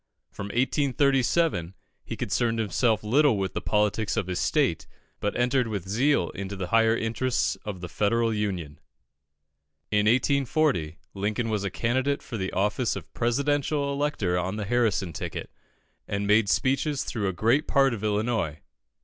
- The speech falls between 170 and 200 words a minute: No, average, 155 wpm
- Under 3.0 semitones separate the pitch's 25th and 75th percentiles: No, average, 4.6 semitones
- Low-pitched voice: Yes, low, 110 Hz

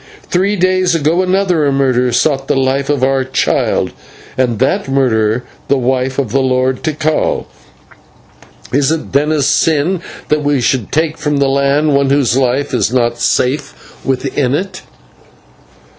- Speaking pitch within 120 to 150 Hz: Yes, medium, 140 Hz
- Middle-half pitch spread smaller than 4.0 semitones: Yes, average, 2.8 semitones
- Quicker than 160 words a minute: No, average, 150 wpm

